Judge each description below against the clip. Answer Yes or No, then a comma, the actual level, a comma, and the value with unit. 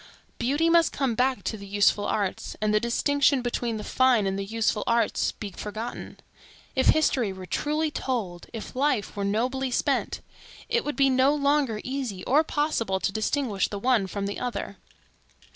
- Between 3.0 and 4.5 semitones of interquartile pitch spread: No, average, 4.9 semitones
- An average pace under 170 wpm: No, average, 175 wpm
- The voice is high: Yes, high, 240 Hz